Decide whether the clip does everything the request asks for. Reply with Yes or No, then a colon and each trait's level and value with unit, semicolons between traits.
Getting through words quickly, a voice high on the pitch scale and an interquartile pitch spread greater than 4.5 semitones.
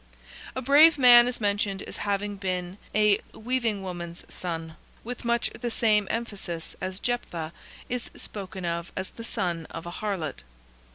No: average, 155 wpm; high, 200 Hz; average, 5.1 semitones